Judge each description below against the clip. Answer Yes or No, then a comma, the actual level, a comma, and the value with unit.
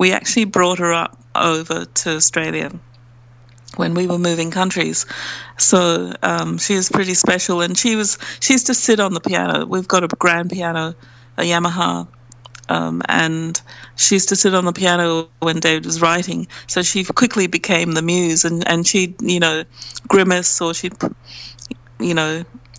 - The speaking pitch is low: No, medium, 170 Hz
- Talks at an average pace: Yes, average, 170 wpm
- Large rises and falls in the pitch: Yes, wide, 6.7 semitones